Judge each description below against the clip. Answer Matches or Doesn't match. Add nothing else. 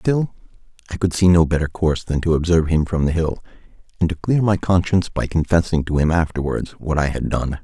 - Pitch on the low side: Matches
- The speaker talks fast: Matches